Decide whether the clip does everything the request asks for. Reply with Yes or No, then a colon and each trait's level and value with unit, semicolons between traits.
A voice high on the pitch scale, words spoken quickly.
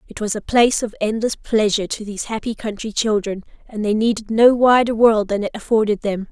Yes: high, 215 Hz; fast, 210 wpm